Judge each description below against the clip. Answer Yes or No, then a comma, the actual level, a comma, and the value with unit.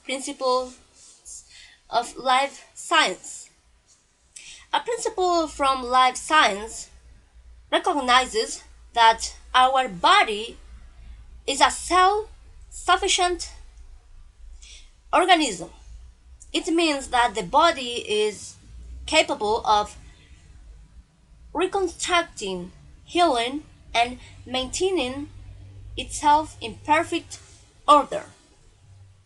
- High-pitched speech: Yes, very high, 255 Hz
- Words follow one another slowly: Yes, slow, 70 wpm